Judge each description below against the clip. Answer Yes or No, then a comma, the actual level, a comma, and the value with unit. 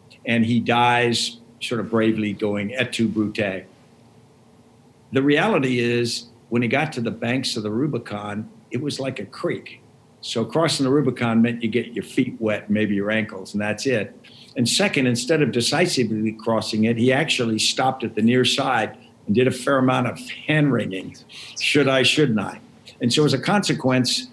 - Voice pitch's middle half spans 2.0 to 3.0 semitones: Yes, average, 2.7 semitones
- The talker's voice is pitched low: Yes, low, 120 Hz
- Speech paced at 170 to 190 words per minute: Yes, average, 185 wpm